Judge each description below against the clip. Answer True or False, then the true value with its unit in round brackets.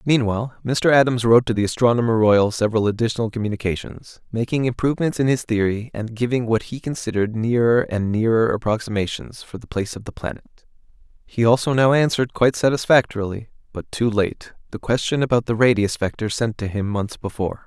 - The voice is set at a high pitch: False (115 Hz)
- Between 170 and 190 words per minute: True (175 wpm)